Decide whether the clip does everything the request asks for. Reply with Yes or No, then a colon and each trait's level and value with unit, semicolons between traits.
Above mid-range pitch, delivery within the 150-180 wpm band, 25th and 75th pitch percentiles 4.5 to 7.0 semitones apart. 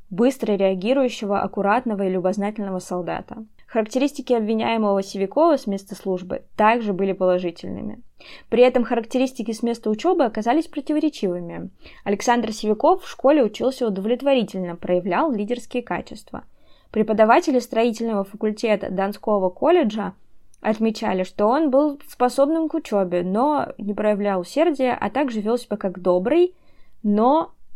No: high, 220 Hz; average, 120 wpm; average, 4.8 semitones